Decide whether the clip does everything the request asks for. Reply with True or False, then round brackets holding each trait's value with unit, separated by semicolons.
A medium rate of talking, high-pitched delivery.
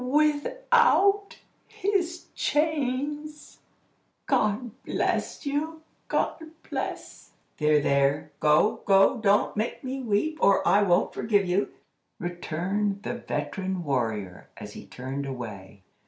False (110 wpm; 205 Hz)